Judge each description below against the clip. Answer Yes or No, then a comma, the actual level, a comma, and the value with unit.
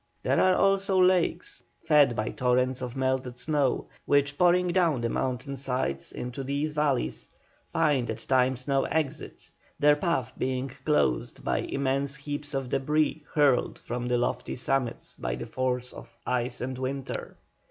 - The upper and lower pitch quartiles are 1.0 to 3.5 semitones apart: Yes, average, 2.9 semitones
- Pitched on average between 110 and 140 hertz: Yes, low, 135 Hz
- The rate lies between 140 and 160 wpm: Yes, average, 155 wpm